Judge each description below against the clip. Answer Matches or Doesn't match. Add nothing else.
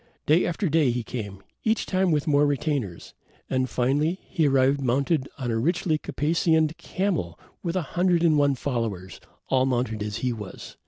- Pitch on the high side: Doesn't match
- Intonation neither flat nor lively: Matches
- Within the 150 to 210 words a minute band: Matches